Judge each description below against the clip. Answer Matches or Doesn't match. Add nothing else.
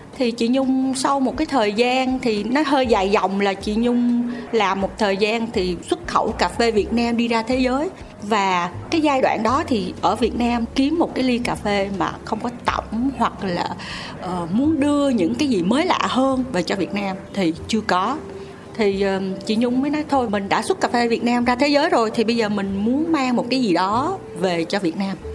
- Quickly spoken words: Doesn't match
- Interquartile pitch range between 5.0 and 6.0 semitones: Doesn't match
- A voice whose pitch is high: Matches